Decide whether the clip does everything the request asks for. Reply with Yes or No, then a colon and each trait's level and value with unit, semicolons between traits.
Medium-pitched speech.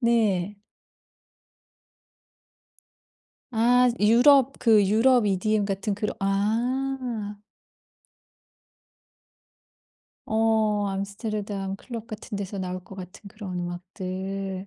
No: high, 210 Hz